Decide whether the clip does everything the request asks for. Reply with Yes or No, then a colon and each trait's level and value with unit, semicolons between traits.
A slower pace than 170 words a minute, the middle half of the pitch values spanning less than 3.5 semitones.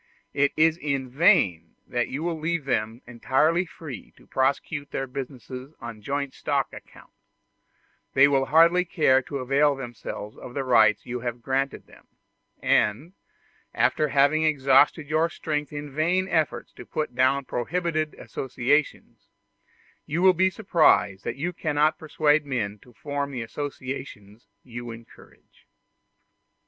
No: average, 140 wpm; average, 4.0 semitones